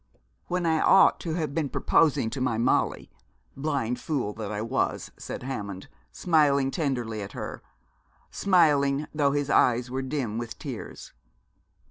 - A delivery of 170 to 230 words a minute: No, average, 145 wpm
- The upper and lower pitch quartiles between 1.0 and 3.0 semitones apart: No, average, 4.5 semitones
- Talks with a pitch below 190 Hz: Yes, low, 135 Hz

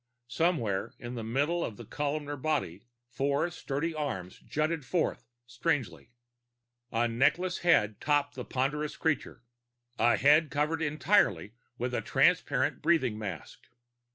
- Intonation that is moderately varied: Yes, average, 4.8 semitones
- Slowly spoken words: Yes, slow, 125 wpm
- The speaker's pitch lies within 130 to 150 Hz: Yes, medium, 140 Hz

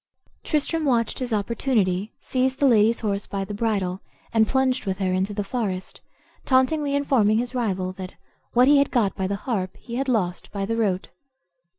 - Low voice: No, high, 220 Hz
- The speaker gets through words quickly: No, average, 185 wpm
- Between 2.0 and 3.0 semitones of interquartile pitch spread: No, average, 4.8 semitones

